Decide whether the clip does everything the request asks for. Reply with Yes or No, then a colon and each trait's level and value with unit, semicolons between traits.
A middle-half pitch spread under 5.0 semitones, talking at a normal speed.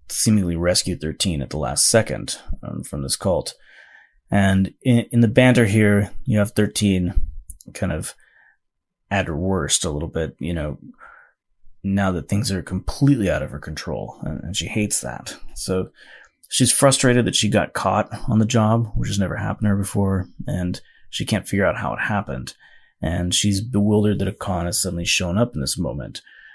Yes: average, 3.6 semitones; average, 185 wpm